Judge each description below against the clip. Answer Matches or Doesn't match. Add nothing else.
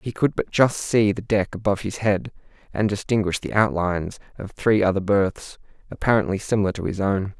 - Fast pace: Doesn't match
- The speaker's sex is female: Doesn't match